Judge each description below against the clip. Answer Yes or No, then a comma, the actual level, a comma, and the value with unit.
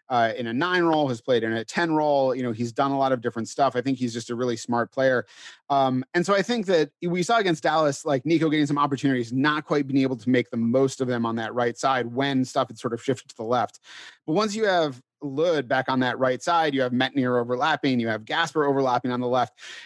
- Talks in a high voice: No, low, 135 Hz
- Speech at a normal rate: No, fast, 265 wpm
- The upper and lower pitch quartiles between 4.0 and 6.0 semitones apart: No, average, 3.4 semitones